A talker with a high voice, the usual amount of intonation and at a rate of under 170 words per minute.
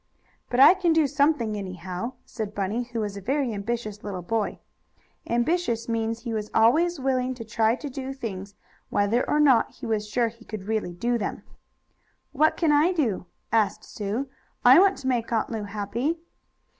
No: high, 230 Hz; average, 4.2 semitones; average, 180 wpm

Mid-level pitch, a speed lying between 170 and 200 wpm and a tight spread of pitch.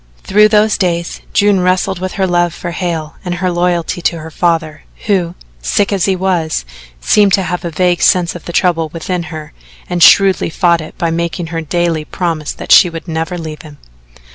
Yes: medium, 175 Hz; average, 195 wpm; narrow, 2.1 semitones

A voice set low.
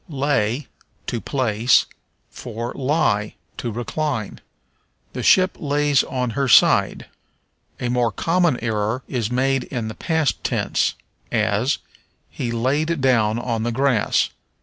Yes: low, 125 Hz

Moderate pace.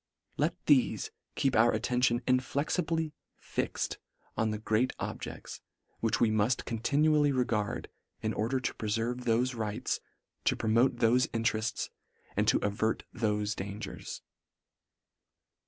No: slow, 120 wpm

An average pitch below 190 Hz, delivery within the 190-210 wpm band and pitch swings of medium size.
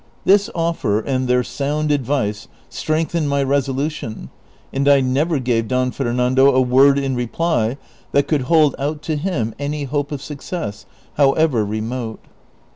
No: medium, 140 Hz; average, 145 wpm; average, 3.1 semitones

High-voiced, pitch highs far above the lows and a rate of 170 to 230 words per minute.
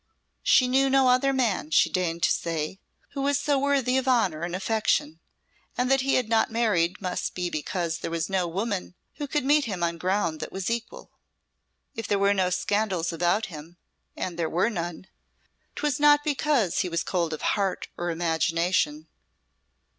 Yes: high, 195 Hz; wide, 6.9 semitones; average, 180 wpm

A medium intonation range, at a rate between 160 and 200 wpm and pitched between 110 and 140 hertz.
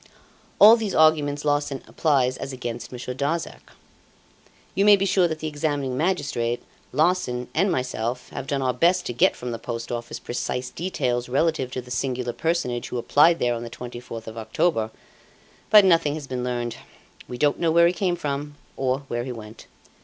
Yes: average, 4.9 semitones; average, 185 wpm; low, 135 Hz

